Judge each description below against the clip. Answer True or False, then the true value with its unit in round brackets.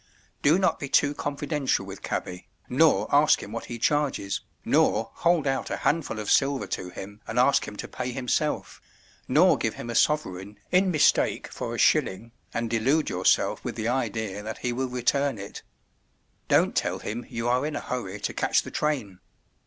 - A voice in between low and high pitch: False (125 Hz)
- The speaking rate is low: False (185 wpm)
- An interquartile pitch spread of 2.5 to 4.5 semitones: False (5.1 semitones)